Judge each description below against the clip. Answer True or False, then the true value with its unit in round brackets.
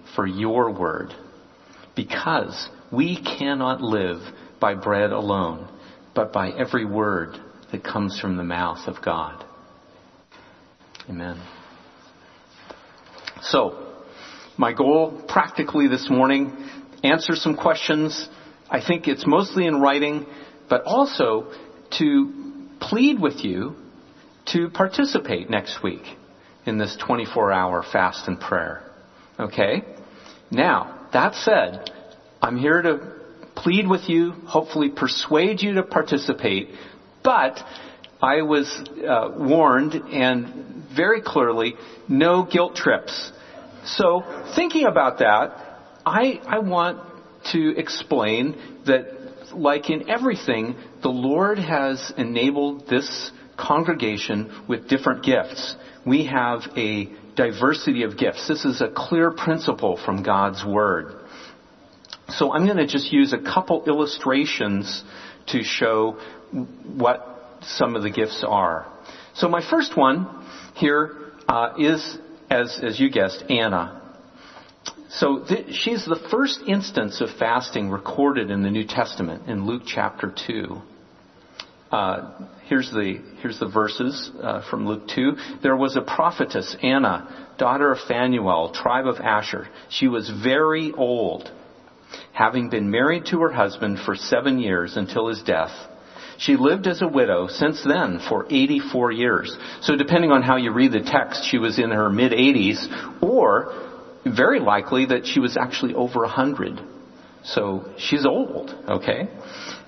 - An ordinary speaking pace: False (130 wpm)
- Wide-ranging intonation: True (6.8 semitones)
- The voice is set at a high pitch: False (140 Hz)